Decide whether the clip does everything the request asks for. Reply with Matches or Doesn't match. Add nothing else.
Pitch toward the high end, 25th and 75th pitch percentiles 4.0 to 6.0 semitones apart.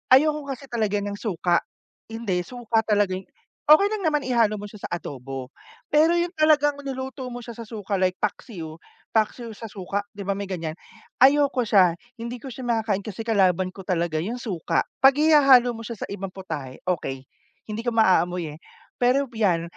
Matches